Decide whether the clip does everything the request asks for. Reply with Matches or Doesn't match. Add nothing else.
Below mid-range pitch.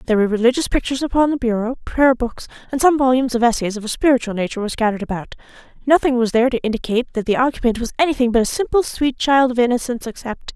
Doesn't match